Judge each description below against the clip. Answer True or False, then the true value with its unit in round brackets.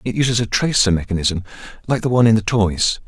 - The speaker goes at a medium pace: False (215 wpm)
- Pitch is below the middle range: True (110 Hz)